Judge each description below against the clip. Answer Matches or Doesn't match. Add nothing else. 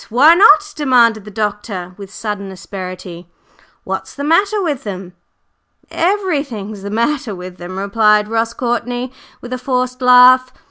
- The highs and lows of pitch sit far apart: Doesn't match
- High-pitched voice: Matches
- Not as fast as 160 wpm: Matches